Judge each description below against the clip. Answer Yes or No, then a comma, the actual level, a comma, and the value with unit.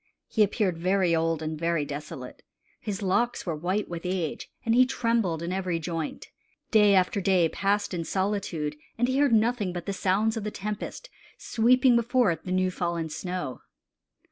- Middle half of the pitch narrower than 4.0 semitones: No, average, 4.3 semitones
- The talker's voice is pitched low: No, medium, 185 Hz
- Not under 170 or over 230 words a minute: Yes, average, 175 wpm